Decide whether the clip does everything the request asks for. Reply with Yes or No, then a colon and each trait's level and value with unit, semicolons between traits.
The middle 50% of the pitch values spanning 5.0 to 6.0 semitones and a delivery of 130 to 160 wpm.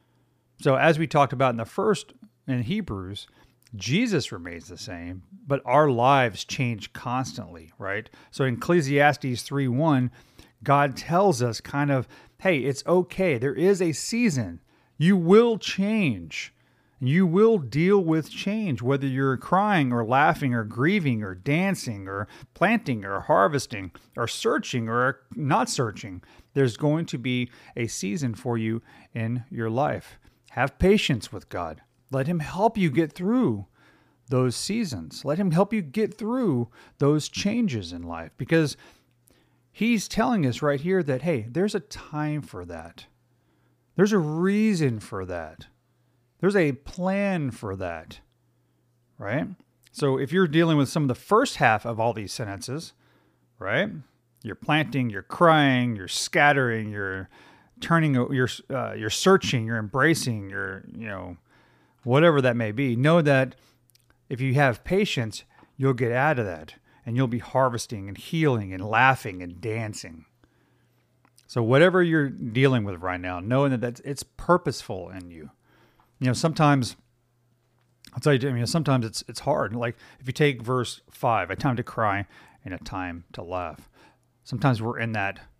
Yes: wide, 5.4 semitones; average, 155 wpm